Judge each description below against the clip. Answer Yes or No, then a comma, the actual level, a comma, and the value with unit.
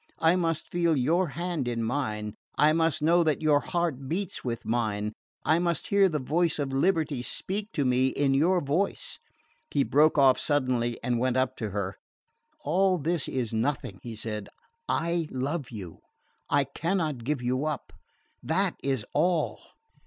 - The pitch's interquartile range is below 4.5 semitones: No, average, 5.2 semitones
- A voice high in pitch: No, medium, 145 Hz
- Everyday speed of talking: Yes, average, 165 wpm